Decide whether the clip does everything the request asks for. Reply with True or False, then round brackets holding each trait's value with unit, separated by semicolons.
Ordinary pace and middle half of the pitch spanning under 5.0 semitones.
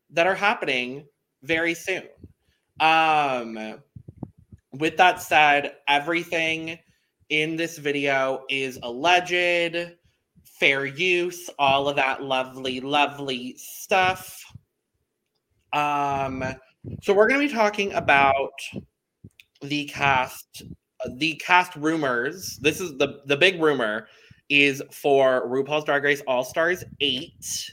False (110 wpm; 3.8 semitones)